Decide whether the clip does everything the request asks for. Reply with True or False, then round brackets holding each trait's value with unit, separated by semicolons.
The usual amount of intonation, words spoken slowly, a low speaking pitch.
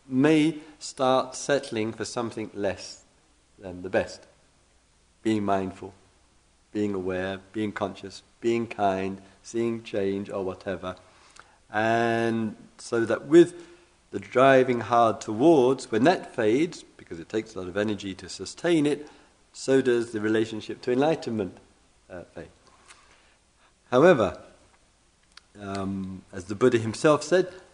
True (4.5 semitones; 125 wpm; 105 Hz)